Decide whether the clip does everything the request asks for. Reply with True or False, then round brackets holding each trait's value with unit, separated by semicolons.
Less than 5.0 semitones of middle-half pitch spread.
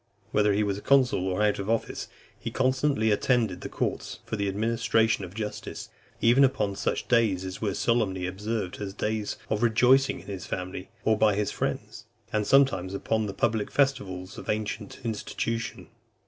True (2.8 semitones)